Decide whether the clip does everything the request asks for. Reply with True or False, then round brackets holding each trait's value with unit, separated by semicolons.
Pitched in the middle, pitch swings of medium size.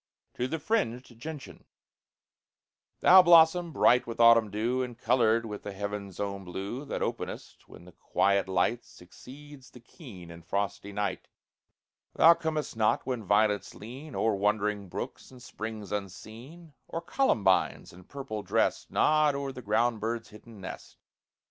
False (115 Hz; 4.8 semitones)